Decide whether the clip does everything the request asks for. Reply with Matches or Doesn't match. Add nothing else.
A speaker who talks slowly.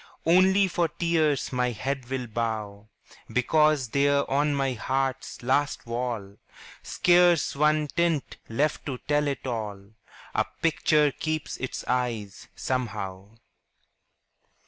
Matches